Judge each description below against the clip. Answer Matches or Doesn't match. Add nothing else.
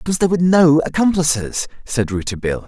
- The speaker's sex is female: Doesn't match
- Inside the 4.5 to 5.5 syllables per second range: Doesn't match